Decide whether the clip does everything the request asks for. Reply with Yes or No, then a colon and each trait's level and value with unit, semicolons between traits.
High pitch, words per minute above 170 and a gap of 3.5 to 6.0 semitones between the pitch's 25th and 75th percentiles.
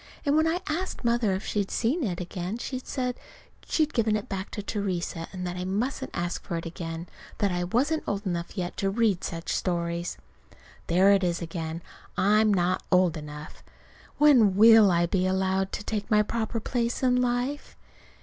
Yes: high, 195 Hz; average, 180 wpm; average, 4.8 semitones